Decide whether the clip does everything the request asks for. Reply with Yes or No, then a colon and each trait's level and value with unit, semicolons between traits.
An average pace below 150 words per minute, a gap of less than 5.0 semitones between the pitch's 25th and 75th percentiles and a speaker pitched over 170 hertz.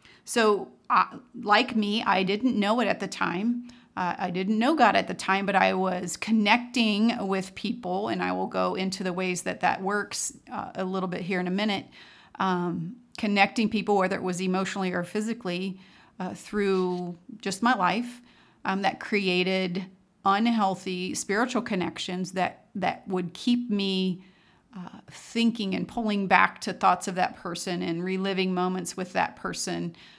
No: average, 165 wpm; average, 2.8 semitones; high, 190 Hz